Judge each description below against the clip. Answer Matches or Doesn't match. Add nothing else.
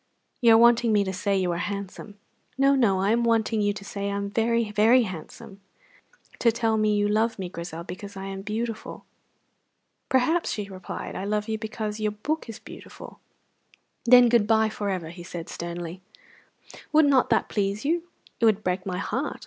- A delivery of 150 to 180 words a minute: Doesn't match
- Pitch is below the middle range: Doesn't match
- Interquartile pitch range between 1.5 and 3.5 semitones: Matches